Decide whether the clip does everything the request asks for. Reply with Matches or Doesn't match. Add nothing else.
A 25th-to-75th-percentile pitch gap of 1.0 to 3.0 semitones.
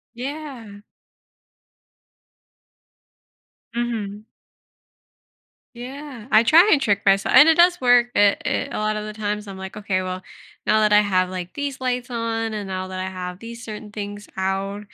Doesn't match